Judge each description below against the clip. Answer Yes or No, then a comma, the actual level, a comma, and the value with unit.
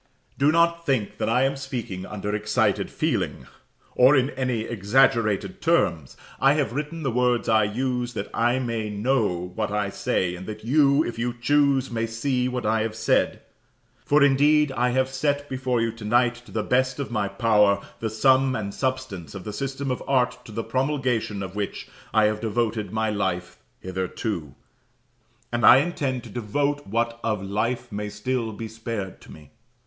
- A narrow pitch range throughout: No, average, 3.9 semitones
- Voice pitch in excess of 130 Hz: No, low, 120 Hz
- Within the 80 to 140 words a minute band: No, average, 175 wpm